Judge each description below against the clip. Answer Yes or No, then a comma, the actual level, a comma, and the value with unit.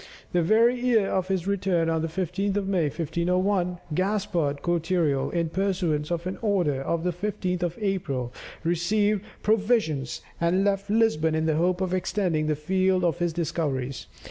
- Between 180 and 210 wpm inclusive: No, average, 165 wpm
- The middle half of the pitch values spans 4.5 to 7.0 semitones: No, average, 3.3 semitones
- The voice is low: No, medium, 180 Hz